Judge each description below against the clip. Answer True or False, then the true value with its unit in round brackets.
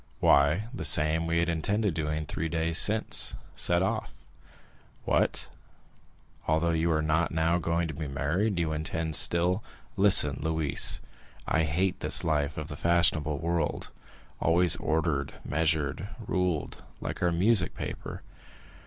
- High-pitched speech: False (80 Hz)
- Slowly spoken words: True (130 wpm)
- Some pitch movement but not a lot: False (2.0 semitones)